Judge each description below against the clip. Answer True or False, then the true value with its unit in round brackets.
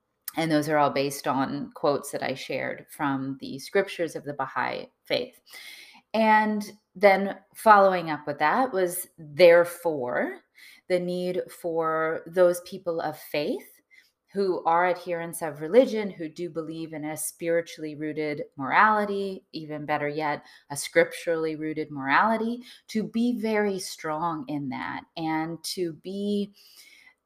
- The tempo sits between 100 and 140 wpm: True (135 wpm)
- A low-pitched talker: False (170 Hz)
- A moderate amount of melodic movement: True (4.3 semitones)